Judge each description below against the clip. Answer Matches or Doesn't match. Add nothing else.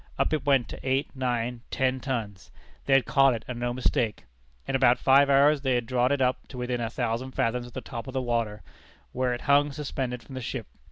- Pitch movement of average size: Doesn't match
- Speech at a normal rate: Doesn't match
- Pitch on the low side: Matches